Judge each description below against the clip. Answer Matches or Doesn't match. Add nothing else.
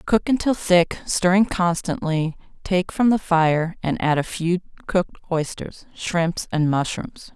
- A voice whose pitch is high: Doesn't match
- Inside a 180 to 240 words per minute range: Doesn't match